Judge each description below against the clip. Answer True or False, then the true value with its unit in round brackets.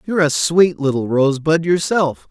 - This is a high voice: False (160 Hz)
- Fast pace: False (155 wpm)